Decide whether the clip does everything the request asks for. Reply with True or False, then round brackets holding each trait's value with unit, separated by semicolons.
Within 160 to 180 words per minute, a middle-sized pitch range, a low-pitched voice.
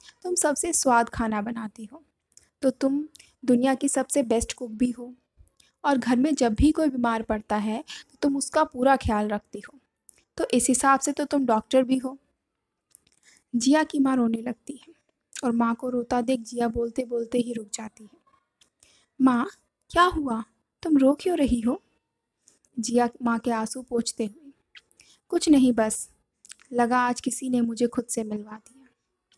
False (170 wpm; 3.2 semitones; 250 Hz)